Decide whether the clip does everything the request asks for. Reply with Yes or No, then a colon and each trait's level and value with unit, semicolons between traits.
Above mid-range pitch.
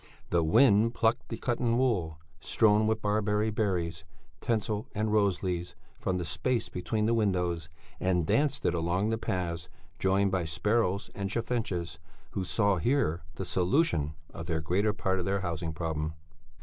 No: very low, 95 Hz